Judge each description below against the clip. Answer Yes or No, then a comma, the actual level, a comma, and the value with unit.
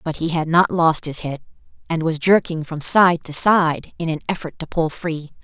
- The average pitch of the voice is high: No, medium, 165 Hz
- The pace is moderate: No, fast, 220 wpm